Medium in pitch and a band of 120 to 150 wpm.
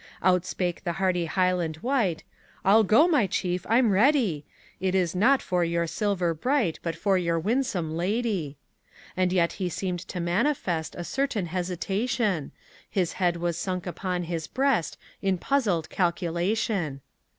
Yes: medium, 180 Hz; average, 145 wpm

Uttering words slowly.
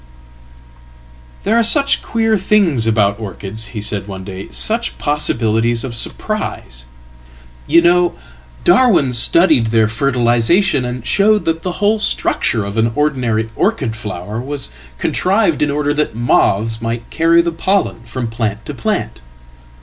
Yes: slow, 130 wpm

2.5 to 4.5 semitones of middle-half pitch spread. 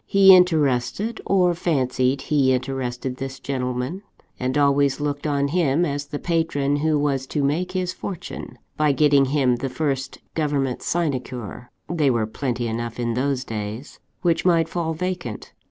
Yes: average, 4.1 semitones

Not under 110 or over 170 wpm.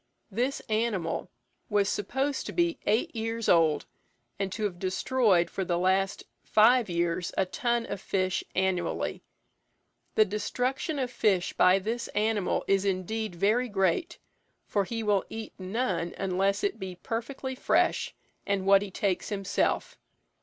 Yes: average, 145 wpm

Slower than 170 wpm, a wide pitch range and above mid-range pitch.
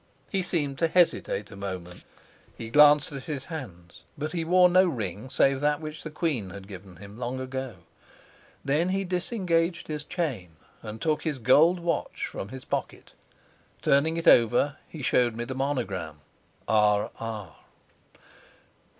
No: average, 155 wpm; wide, 7.2 semitones; low, 135 Hz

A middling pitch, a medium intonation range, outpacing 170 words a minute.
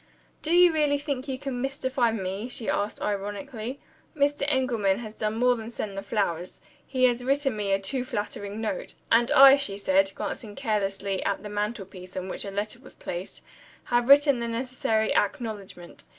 No: high, 225 Hz; average, 4.5 semitones; average, 180 wpm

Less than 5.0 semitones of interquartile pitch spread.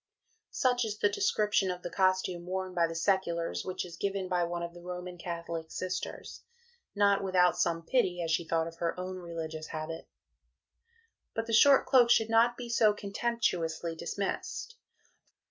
Yes: average, 3.5 semitones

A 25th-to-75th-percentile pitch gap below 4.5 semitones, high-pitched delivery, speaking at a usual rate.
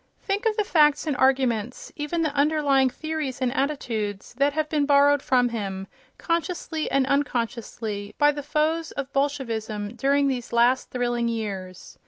Yes: average, 4.1 semitones; very high, 275 Hz; average, 155 wpm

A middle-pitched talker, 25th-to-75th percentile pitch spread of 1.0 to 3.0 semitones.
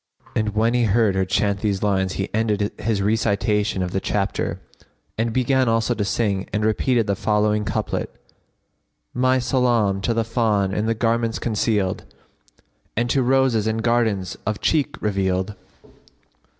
No: low, 110 Hz; narrow, 2.6 semitones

